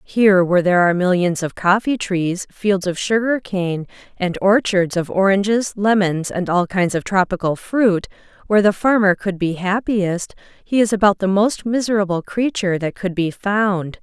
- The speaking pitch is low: No, high, 195 Hz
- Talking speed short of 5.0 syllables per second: Yes, 4.8 syllables/s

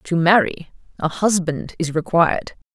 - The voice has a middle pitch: Yes, medium, 170 Hz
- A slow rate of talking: Yes, slow, 130 wpm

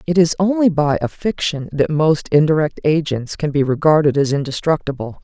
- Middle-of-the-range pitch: Yes, medium, 155 Hz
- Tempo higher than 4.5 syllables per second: Yes, 5.2 syllables/s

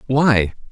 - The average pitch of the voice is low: Yes, low, 115 Hz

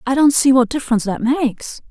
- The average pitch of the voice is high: Yes, very high, 255 Hz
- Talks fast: Yes, fast, 220 wpm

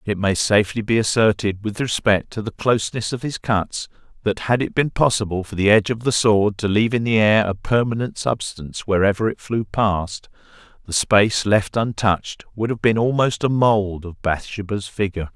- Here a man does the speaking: Yes, male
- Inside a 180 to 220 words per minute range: Yes, average, 190 wpm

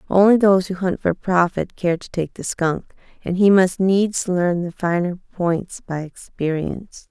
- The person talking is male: No, female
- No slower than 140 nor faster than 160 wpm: No, average, 175 wpm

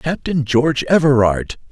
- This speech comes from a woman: No, male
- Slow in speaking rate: Yes, slow, 105 wpm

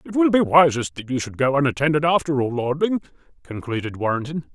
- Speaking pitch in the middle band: Yes, medium, 145 Hz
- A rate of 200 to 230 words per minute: No, average, 185 wpm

